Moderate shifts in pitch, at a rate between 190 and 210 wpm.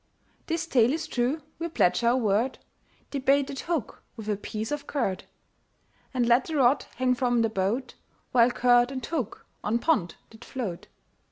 No: average, 3.6 semitones; average, 170 wpm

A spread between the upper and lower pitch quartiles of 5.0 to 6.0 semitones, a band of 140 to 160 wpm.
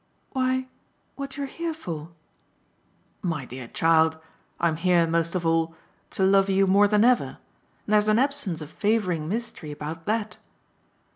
Yes: wide, 5.6 semitones; average, 150 wpm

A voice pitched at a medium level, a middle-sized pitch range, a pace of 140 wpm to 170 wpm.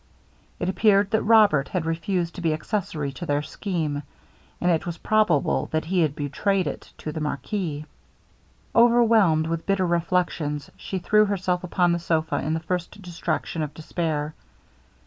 Yes: medium, 170 Hz; average, 3.6 semitones; average, 160 wpm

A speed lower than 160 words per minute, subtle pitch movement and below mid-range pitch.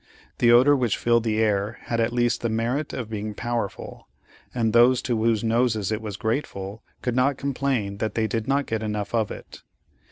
No: average, 195 wpm; narrow, 2.1 semitones; low, 115 Hz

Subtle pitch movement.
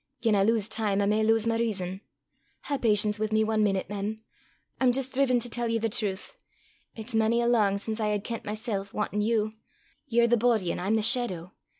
Yes: narrow, 2.1 semitones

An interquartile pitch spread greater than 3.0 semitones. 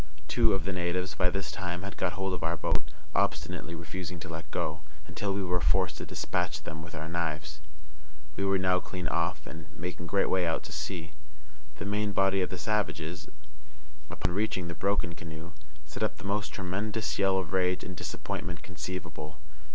No: narrow, 2.6 semitones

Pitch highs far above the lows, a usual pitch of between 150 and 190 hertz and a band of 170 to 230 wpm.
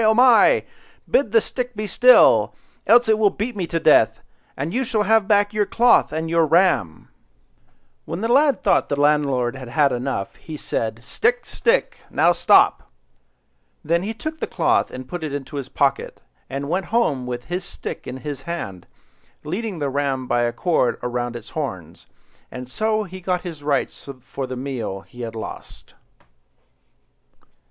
Yes: wide, 8.7 semitones; medium, 155 Hz; average, 175 wpm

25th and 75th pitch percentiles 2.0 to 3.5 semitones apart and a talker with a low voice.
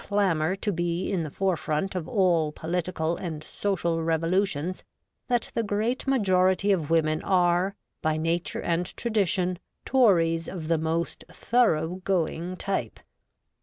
No: average, 3.1 semitones; medium, 175 Hz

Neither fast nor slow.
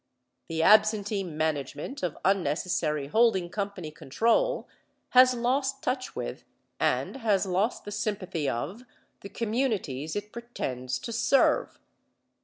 No: slow, 115 wpm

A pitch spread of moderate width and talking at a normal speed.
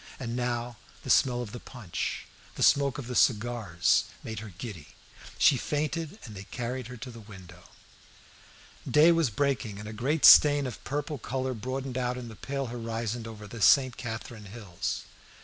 Yes: average, 3.4 semitones; average, 175 wpm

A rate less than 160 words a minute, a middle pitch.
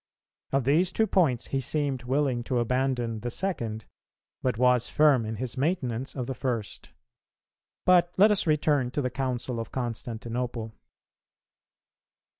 No: average, 140 wpm; low, 130 Hz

